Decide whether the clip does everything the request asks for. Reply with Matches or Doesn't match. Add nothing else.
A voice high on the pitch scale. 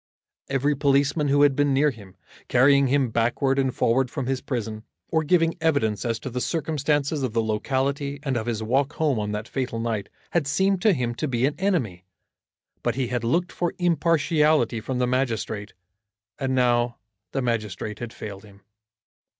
Doesn't match